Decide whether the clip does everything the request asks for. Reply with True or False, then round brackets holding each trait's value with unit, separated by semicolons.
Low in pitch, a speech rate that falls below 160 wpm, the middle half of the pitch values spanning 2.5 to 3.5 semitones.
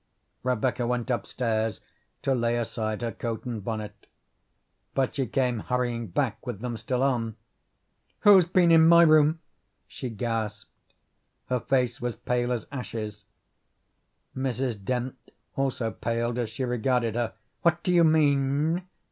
True (125 Hz; 140 wpm; 2.9 semitones)